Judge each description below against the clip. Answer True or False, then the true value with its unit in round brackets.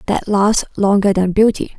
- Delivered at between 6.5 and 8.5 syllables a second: False (4.6 syllables/s)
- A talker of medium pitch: False (200 Hz)